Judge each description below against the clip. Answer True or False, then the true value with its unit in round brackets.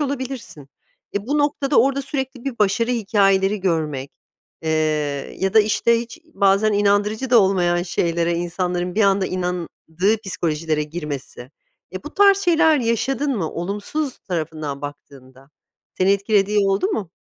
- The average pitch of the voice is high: True (195 Hz)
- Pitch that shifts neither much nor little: False (5.8 semitones)